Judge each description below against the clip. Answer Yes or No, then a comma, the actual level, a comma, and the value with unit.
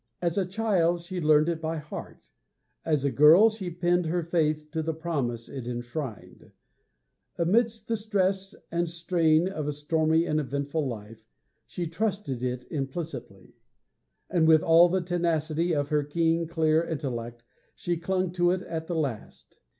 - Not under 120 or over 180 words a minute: Yes, average, 160 wpm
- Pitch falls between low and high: Yes, medium, 160 Hz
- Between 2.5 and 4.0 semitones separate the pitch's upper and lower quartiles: Yes, average, 3.0 semitones